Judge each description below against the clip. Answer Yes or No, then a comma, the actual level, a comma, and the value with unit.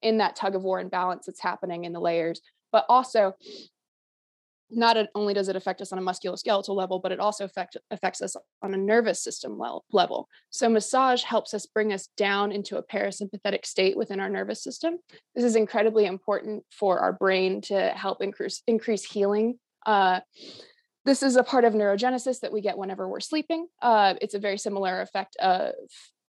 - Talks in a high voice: Yes, high, 205 Hz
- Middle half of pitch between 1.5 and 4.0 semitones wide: Yes, average, 3.4 semitones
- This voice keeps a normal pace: Yes, average, 185 wpm